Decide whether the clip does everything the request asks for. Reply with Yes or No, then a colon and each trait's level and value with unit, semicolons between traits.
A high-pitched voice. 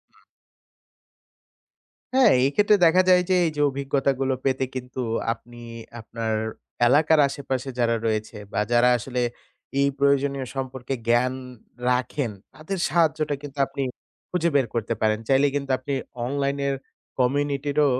No: low, 135 Hz